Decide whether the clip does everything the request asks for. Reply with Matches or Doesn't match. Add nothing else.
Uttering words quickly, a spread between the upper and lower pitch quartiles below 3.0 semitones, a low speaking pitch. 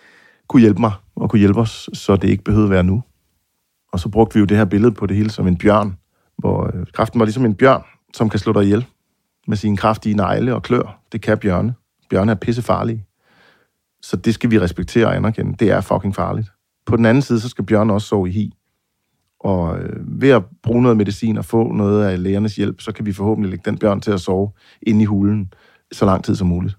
Matches